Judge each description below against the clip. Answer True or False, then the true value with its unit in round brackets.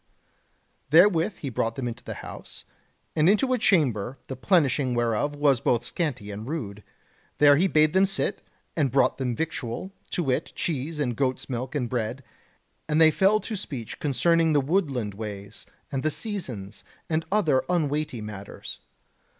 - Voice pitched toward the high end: False (140 Hz)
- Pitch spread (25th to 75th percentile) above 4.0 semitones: True (5.3 semitones)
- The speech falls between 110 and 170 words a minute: True (160 wpm)